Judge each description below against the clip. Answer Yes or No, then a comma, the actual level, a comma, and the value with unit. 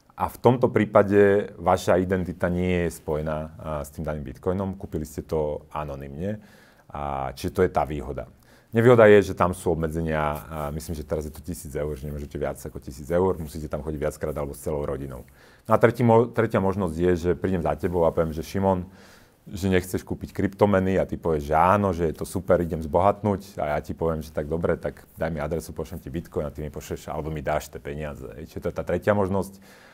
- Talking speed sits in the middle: No, fast, 225 wpm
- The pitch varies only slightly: No, average, 4.2 semitones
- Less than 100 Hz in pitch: Yes, very low, 85 Hz